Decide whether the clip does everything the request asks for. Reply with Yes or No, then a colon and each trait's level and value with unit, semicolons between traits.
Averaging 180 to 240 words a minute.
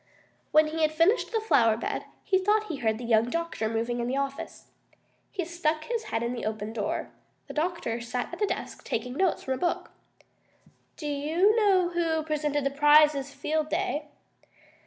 Yes: average, 185 wpm